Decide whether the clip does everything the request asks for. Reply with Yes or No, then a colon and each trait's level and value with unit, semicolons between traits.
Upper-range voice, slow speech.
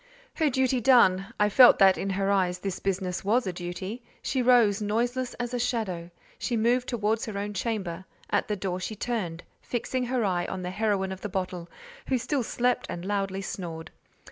No: high, 205 Hz; average, 185 wpm